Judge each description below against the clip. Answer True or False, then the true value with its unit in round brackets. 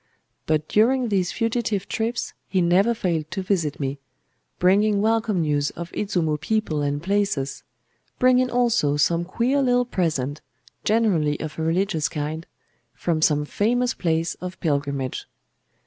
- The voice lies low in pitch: False (175 Hz)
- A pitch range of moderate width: False (6.3 semitones)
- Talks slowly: True (130 wpm)